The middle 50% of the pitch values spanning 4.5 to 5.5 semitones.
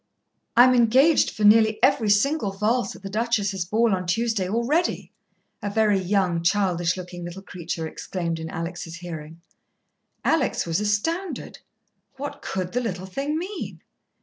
Yes: average, 4.9 semitones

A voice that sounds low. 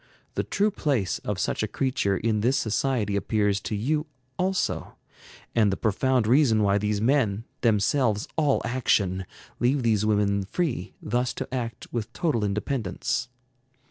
Yes: low, 115 Hz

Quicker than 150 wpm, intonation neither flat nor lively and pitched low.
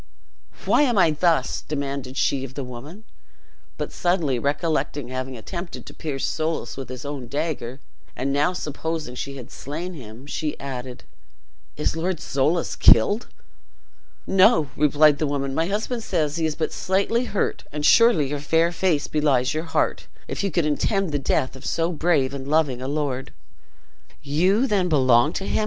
No: average, 170 wpm; average, 4.0 semitones; medium, 150 Hz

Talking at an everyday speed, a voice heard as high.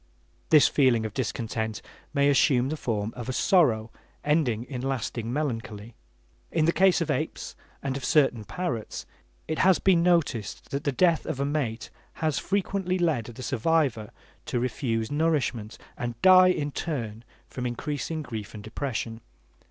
No: average, 155 wpm; low, 135 Hz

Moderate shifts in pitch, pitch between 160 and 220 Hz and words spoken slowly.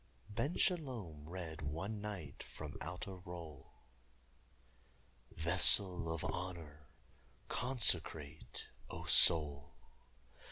No: average, 4.7 semitones; very low, 85 Hz; slow, 85 wpm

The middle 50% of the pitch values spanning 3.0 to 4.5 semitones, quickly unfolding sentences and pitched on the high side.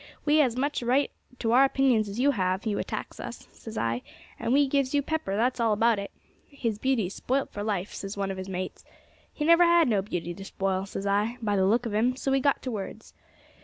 No: average, 5.2 semitones; fast, 240 wpm; high, 225 Hz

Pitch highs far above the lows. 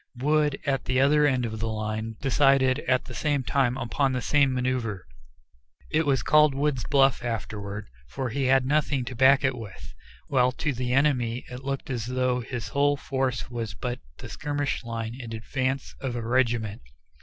No: average, 2.7 semitones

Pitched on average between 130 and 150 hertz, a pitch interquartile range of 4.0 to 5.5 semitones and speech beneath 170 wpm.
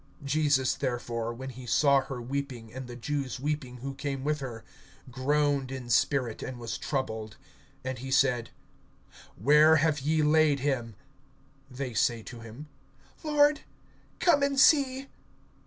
No: low, 135 Hz; average, 3.4 semitones; average, 140 wpm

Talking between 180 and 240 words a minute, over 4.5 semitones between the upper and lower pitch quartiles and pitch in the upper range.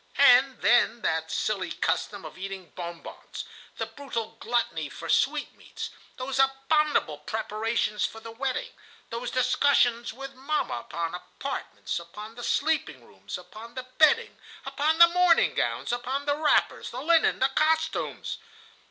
No: average, 145 wpm; average, 5.0 semitones; high, 245 Hz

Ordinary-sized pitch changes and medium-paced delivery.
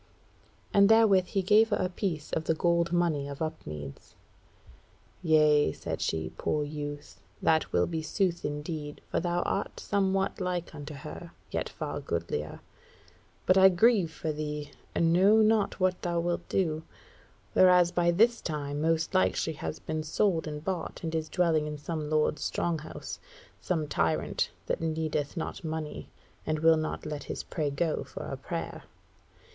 Yes: average, 3.1 semitones; average, 165 wpm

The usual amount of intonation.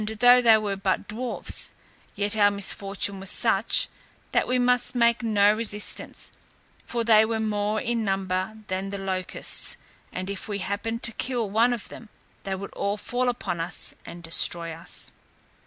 Yes: average, 3.0 semitones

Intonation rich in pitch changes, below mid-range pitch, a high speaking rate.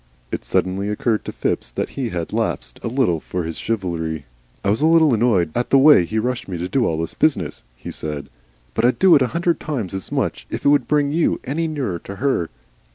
Yes: wide, 8.2 semitones; low, 115 Hz; fast, 225 wpm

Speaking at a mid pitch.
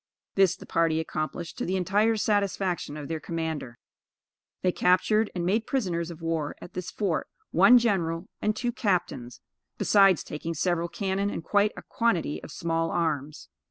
Yes: medium, 175 Hz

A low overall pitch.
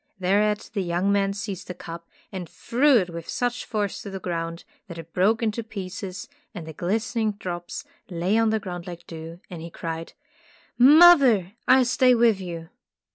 No: high, 195 Hz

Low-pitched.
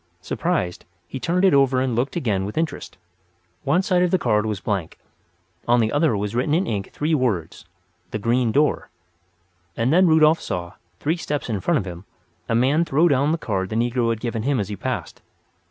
Yes: low, 125 Hz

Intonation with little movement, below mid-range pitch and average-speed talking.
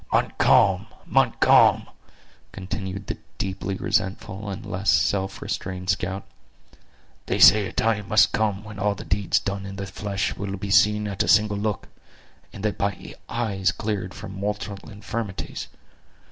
Yes: narrow, 1.5 semitones; low, 100 Hz; average, 145 wpm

